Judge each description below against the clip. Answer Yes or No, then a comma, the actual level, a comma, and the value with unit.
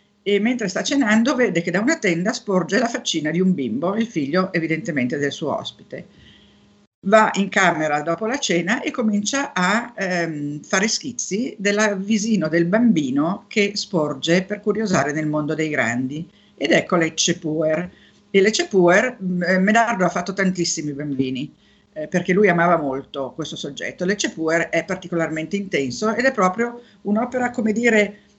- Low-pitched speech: No, medium, 185 Hz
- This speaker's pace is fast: No, average, 160 wpm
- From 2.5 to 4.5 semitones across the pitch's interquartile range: No, average, 4.9 semitones